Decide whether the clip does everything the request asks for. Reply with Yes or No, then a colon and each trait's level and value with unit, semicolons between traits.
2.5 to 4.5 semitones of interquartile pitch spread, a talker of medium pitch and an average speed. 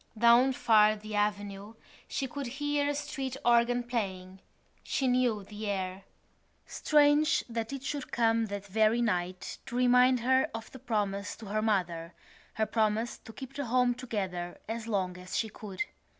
No: average, 3.7 semitones; high, 225 Hz; average, 165 wpm